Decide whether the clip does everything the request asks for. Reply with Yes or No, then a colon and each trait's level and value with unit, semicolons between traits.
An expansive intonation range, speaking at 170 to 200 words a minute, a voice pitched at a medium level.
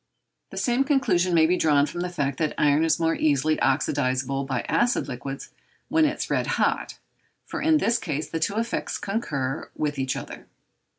Yes: wide, 6.3 semitones; average, 185 wpm; medium, 155 Hz